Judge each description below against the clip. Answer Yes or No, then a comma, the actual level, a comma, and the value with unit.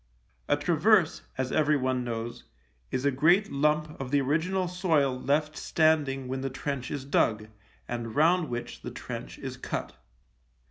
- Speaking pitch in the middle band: Yes, medium, 145 Hz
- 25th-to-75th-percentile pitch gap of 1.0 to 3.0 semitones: No, average, 3.5 semitones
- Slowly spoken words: No, average, 150 wpm